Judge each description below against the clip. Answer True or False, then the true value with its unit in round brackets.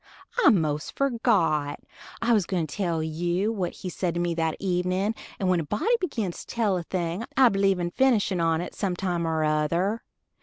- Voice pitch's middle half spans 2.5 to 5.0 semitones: True (3.8 semitones)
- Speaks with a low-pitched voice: False (180 Hz)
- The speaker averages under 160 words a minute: False (195 wpm)